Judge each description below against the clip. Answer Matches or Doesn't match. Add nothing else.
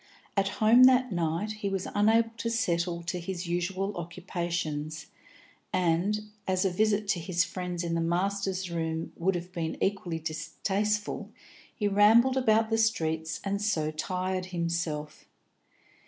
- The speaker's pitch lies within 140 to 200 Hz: Matches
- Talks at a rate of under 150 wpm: Matches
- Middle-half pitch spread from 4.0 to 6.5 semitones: Doesn't match